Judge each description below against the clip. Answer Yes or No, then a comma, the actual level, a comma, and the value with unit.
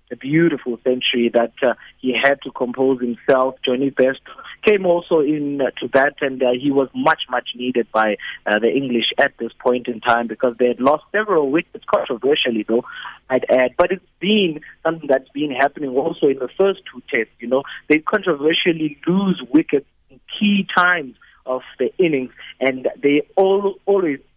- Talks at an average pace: Yes, average, 180 wpm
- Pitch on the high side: No, medium, 140 Hz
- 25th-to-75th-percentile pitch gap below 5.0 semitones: No, wide, 5.6 semitones